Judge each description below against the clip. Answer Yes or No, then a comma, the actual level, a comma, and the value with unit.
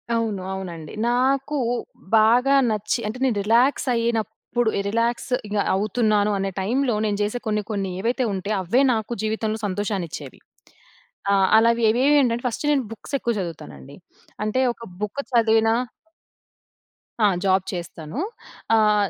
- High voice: Yes, high, 220 Hz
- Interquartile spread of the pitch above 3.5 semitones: No, average, 3.0 semitones